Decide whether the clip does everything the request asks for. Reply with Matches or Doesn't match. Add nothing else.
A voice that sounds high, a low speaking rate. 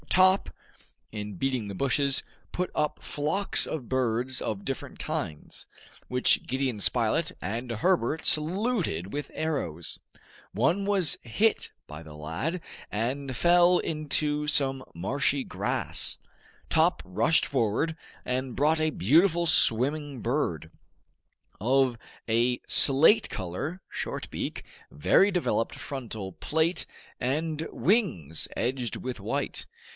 Doesn't match